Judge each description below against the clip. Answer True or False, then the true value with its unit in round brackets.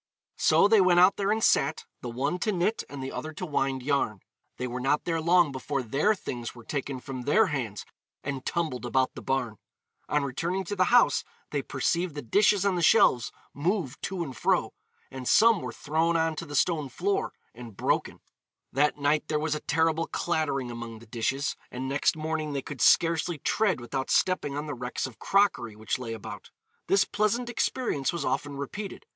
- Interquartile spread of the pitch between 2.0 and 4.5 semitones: False (5.1 semitones)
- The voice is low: False (150 Hz)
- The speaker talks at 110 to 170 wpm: False (195 wpm)